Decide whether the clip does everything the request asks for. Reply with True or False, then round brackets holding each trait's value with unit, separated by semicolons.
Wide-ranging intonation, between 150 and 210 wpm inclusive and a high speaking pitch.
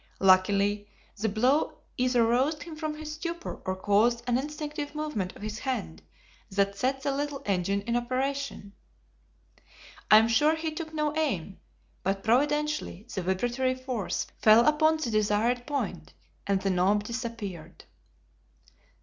False (6.6 semitones; 140 wpm; 240 Hz)